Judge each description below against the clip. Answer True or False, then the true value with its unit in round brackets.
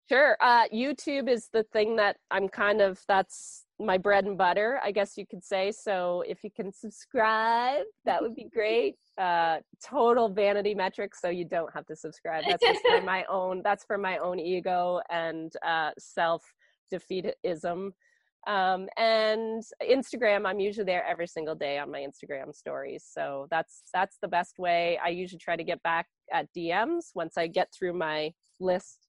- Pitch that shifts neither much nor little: True (4.1 semitones)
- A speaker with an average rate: True (170 wpm)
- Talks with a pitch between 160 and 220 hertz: True (190 Hz)